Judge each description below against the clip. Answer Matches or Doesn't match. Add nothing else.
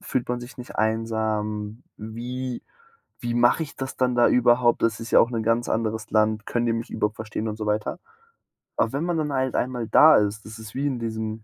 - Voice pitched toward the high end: Doesn't match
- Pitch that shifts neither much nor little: Doesn't match